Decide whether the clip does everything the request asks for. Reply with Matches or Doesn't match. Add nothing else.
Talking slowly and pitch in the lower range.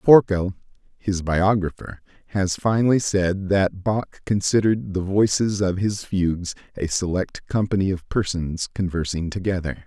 Matches